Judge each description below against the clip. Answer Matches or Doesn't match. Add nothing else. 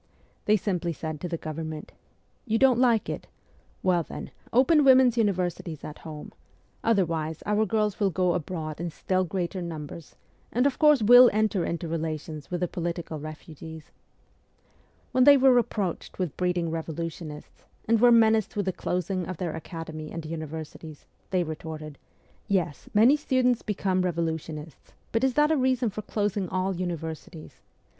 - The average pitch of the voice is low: Doesn't match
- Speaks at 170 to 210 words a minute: Doesn't match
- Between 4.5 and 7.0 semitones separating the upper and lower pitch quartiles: Matches